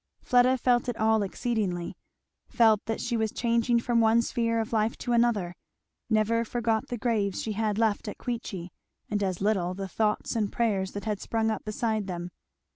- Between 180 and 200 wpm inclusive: Yes, average, 185 wpm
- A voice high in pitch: Yes, high, 220 Hz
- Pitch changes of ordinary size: No, narrow, 2.3 semitones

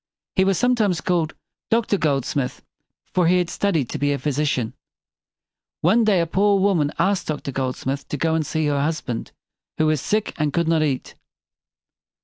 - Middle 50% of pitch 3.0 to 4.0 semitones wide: No, average, 4.8 semitones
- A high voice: No, medium, 160 Hz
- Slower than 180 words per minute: No, average, 185 wpm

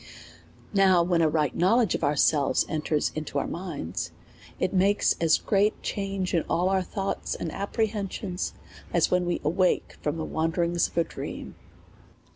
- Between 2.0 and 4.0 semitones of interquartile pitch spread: Yes, average, 3.4 semitones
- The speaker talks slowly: No, average, 160 wpm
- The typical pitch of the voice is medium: Yes, medium, 175 Hz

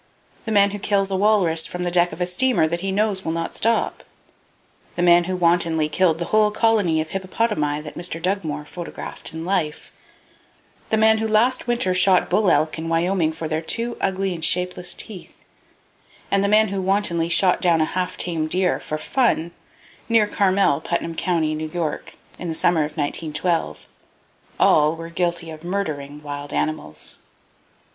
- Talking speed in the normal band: Yes, average, 175 wpm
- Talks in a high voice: No, medium, 175 Hz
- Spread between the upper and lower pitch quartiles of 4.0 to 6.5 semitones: No, average, 3.5 semitones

